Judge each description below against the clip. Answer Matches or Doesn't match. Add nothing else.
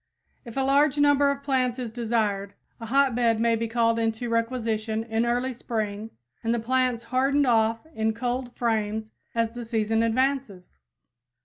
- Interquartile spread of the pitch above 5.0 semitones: Doesn't match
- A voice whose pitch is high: Matches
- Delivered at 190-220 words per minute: Doesn't match